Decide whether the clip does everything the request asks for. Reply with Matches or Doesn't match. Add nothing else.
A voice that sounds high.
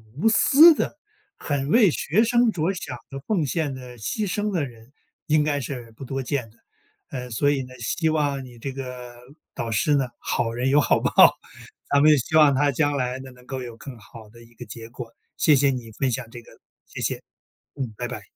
Doesn't match